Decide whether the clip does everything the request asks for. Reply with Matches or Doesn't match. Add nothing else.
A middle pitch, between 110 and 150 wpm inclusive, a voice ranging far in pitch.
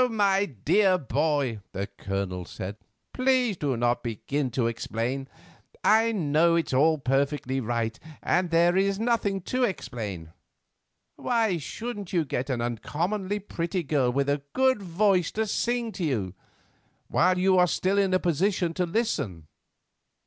Matches